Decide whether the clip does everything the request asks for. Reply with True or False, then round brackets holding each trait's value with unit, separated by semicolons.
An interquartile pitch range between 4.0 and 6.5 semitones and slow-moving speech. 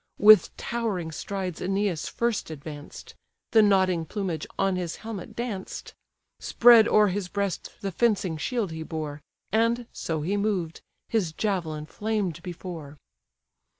True (4.7 semitones; 130 wpm)